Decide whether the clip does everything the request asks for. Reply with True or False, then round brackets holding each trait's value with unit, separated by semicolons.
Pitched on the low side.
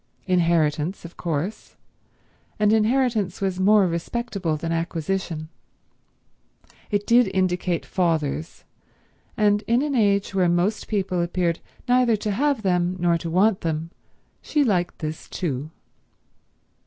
False (185 Hz)